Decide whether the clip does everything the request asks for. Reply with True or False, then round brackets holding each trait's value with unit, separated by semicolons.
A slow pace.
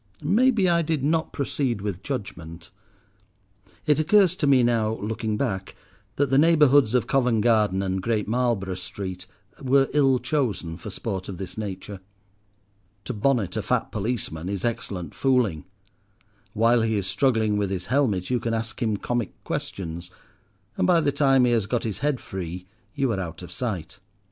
False (170 wpm)